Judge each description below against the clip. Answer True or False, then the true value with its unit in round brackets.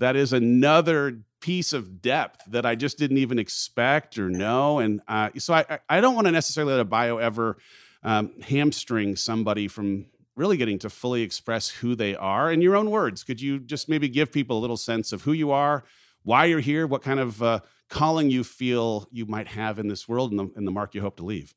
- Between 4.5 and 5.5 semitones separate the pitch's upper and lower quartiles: True (5.1 semitones)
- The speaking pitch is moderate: False (120 Hz)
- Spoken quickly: True (225 wpm)